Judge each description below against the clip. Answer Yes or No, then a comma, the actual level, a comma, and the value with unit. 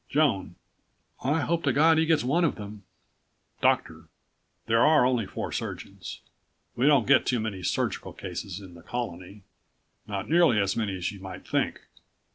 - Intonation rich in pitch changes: Yes, wide, 7.3 semitones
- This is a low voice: Yes, low, 115 Hz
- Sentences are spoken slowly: No, average, 165 wpm